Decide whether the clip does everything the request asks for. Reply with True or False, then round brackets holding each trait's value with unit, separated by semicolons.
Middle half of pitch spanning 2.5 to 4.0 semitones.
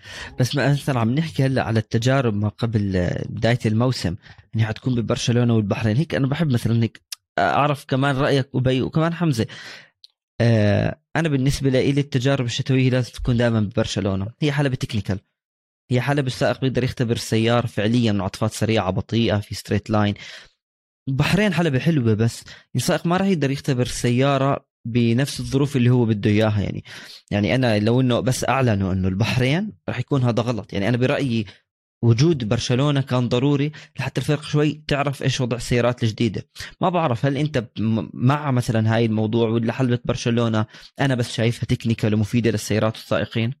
True (3.6 semitones)